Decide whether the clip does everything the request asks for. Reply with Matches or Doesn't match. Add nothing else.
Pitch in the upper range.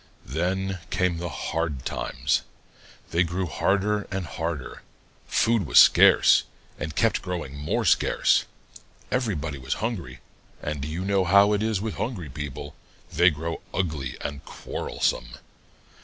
Doesn't match